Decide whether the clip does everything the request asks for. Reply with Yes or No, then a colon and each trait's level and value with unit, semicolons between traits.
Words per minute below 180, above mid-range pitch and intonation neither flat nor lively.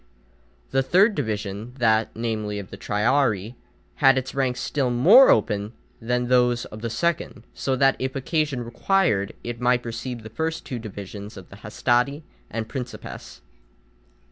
No: average, 150 wpm; low, 120 Hz; average, 3.5 semitones